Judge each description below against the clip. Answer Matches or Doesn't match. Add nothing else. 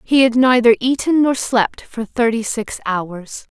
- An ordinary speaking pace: Matches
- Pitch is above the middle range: Matches